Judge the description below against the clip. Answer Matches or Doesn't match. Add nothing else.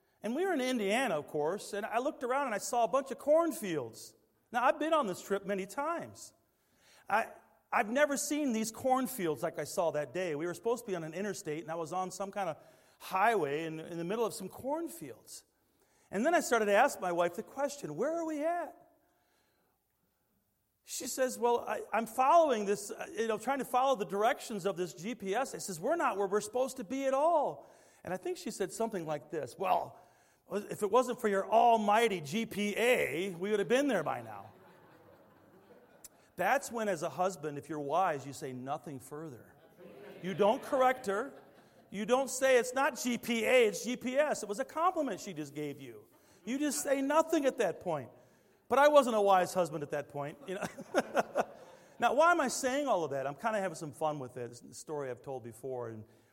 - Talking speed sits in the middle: Doesn't match